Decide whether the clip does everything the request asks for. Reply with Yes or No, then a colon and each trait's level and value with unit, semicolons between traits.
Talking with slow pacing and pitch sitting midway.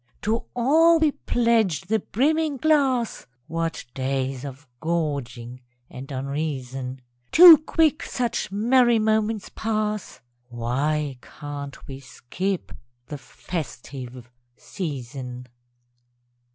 Yes: slow, 100 wpm; medium, 160 Hz